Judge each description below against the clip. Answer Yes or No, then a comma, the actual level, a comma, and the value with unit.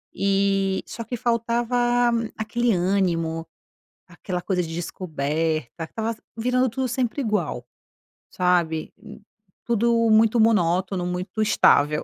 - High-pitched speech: Yes, high, 200 Hz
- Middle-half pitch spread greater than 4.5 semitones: Yes, average, 5.0 semitones